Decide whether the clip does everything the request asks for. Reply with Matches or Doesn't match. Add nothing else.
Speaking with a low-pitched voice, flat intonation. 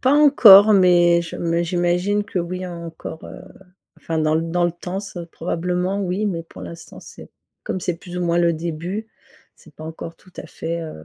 Doesn't match